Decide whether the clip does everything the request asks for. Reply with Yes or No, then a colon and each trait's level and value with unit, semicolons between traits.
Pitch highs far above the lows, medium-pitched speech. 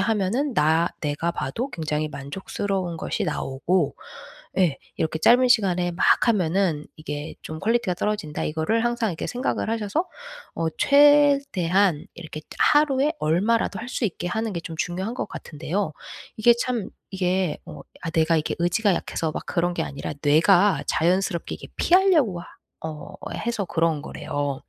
Yes: wide, 6.0 semitones; medium, 180 Hz